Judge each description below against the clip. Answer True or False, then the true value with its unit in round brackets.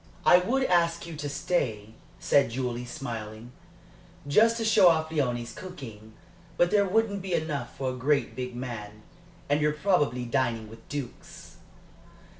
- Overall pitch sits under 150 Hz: True (140 Hz)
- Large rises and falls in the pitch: True (6.5 semitones)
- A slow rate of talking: False (150 wpm)